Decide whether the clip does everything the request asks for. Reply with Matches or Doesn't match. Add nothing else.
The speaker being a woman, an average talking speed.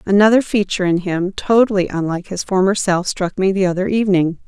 Matches